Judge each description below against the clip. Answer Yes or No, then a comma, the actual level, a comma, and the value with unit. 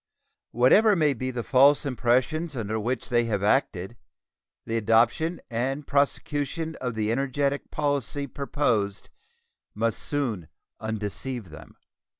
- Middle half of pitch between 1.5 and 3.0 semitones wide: No, average, 4.2 semitones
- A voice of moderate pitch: No, low, 125 Hz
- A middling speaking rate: No, slow, 120 wpm